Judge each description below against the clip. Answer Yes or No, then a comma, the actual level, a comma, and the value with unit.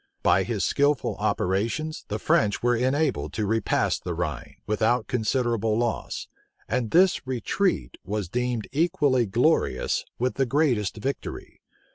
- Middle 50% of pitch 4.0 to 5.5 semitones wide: Yes, average, 4.4 semitones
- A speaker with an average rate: No, slow, 130 wpm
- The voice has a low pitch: Yes, low, 120 Hz